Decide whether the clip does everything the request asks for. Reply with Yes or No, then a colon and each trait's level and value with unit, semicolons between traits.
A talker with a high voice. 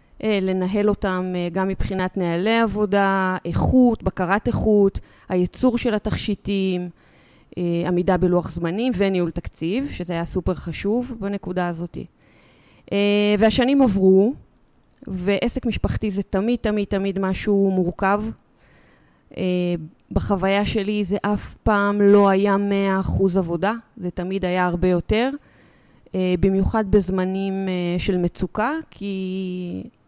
Yes: high, 195 Hz